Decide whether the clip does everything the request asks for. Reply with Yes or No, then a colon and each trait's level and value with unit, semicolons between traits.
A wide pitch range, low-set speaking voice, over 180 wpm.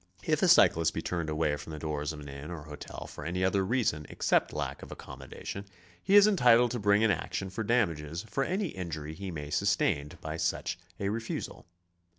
Yes: wide, 6.4 semitones; very low, 85 Hz; fast, 205 wpm